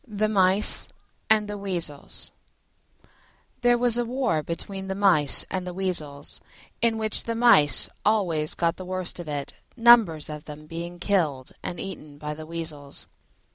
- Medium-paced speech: Yes, average, 150 wpm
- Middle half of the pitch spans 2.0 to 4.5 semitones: No, wide, 5.5 semitones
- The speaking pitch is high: No, medium, 180 Hz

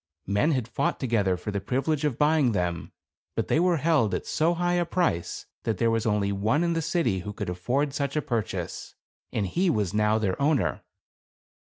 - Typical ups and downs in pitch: No, wide, 7.2 semitones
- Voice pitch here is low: Yes, low, 120 Hz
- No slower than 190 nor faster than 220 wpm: Yes, average, 200 wpm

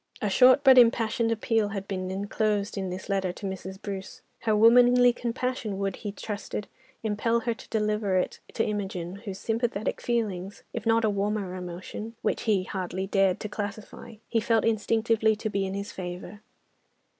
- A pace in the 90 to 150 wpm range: No, average, 170 wpm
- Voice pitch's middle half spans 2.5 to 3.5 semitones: Yes, average, 2.8 semitones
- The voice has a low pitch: No, high, 210 Hz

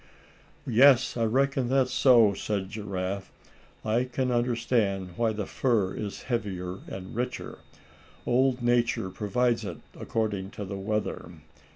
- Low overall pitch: Yes, low, 115 Hz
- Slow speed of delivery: Yes, slow, 130 wpm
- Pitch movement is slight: No, average, 4.0 semitones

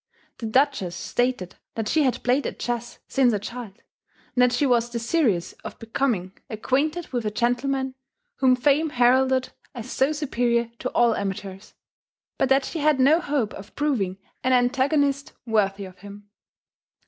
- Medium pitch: No, high, 245 Hz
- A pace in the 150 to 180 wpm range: Yes, average, 160 wpm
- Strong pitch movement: No, average, 3.9 semitones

